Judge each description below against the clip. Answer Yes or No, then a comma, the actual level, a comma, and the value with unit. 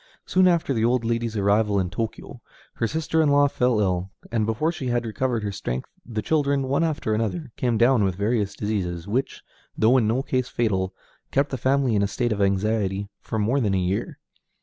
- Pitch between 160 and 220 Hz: No, low, 115 Hz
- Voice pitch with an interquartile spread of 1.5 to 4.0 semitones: No, average, 4.5 semitones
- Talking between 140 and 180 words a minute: No, fast, 205 wpm